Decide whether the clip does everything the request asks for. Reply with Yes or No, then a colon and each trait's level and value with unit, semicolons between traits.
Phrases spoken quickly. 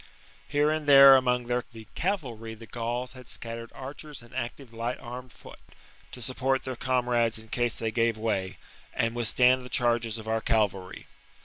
No: average, 170 wpm